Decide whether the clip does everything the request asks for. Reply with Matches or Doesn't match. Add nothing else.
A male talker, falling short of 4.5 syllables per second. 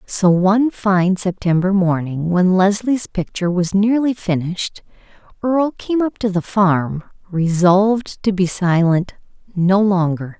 Doesn't match